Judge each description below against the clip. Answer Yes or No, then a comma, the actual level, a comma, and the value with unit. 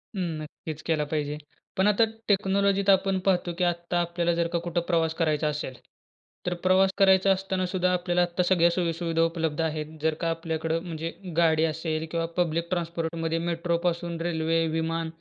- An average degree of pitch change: No, narrow, 1.8 semitones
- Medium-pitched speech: Yes, medium, 170 Hz